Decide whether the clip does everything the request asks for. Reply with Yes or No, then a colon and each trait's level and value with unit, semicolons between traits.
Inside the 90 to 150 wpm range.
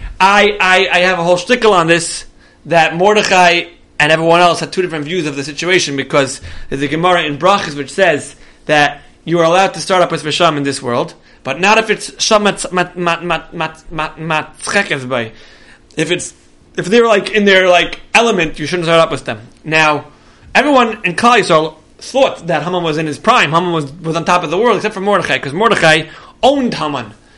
No: average, 190 wpm